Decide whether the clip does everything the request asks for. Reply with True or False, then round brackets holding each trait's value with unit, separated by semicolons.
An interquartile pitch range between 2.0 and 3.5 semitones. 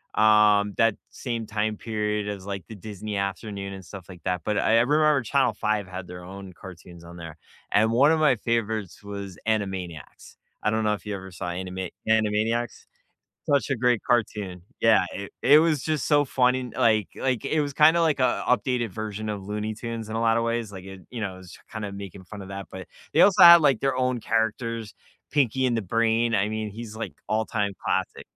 True (3.2 semitones)